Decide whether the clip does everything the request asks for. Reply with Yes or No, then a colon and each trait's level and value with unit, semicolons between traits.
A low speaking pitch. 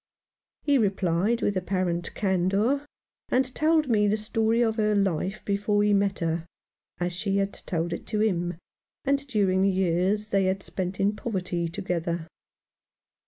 No: high, 195 Hz